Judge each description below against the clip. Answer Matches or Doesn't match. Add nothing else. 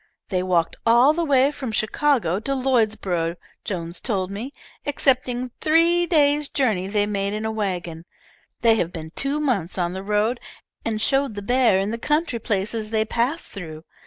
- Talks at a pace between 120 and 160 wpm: Doesn't match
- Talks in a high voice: Matches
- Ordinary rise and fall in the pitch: Doesn't match